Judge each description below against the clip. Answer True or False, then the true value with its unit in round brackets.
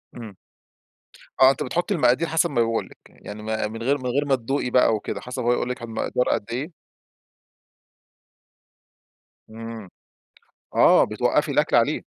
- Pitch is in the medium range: False (125 Hz)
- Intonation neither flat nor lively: True (3.1 semitones)